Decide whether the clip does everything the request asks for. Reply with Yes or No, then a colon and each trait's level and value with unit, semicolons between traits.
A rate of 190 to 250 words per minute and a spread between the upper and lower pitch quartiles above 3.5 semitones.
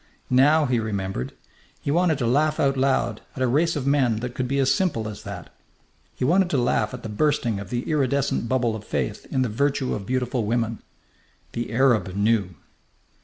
Yes: average, 195 wpm; average, 4.0 semitones